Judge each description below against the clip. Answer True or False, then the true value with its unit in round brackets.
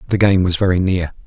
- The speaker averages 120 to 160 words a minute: False (235 wpm)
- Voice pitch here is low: True (95 Hz)